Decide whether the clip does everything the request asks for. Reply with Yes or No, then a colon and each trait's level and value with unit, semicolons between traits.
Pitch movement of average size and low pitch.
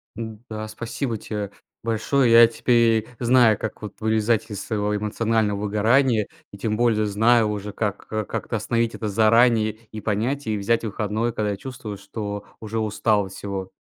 No: narrow, 1.8 semitones; low, 110 Hz